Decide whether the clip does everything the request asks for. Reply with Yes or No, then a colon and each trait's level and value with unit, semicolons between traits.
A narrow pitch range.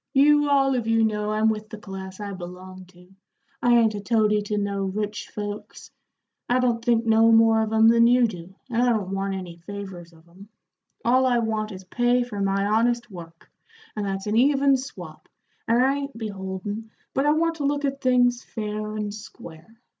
No: average, 3.6 semitones